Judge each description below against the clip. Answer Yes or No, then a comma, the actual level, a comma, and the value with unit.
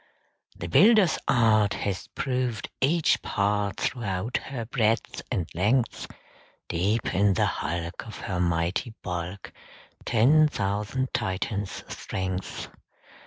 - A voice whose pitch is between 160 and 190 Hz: No, low, 105 Hz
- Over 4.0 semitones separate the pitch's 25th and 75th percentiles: Yes, average, 4.7 semitones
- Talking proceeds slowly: Yes, slow, 110 wpm